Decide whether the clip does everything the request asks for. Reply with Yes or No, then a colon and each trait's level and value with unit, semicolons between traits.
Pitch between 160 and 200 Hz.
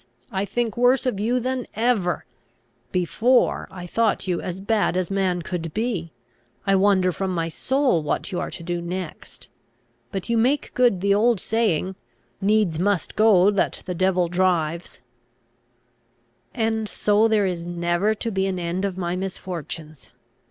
Yes: high, 190 Hz